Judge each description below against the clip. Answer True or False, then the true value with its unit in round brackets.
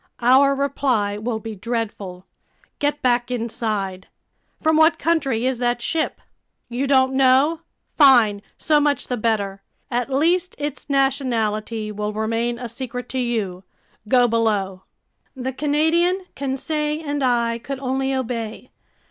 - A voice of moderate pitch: False (250 Hz)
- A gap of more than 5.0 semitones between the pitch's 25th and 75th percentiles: False (3.8 semitones)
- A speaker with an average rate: False (130 wpm)